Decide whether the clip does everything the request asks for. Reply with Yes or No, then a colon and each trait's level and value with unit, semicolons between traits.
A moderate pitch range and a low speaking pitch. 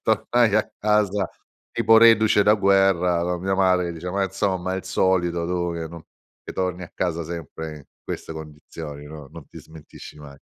Yes: average, 3.0 semitones; very low, 90 Hz